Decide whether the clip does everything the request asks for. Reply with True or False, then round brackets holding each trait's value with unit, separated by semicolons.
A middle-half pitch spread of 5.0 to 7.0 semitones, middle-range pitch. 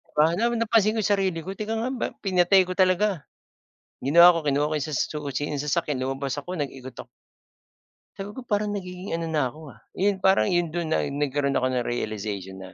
True (5.6 semitones; 165 Hz)